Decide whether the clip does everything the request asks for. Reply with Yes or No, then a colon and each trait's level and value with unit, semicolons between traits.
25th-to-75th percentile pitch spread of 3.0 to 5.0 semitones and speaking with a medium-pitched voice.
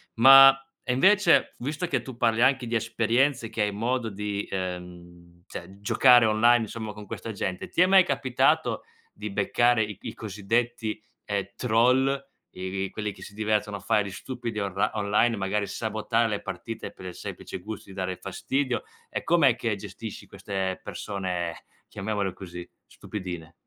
No: average, 3.6 semitones; low, 110 Hz